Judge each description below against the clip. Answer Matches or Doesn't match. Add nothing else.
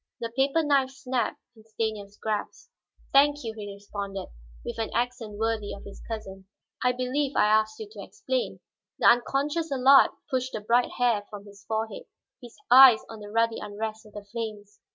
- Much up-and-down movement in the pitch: Doesn't match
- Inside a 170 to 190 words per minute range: Matches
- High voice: Matches